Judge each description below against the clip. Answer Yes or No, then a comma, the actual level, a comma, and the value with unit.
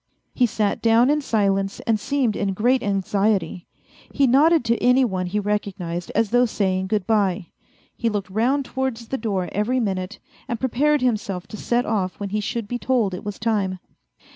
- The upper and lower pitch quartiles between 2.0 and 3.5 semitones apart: No, average, 3.9 semitones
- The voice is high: Yes, high, 215 Hz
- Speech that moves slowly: No, average, 185 wpm